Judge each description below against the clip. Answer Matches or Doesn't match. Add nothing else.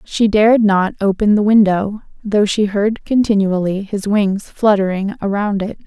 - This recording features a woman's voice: Matches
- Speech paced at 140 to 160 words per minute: Matches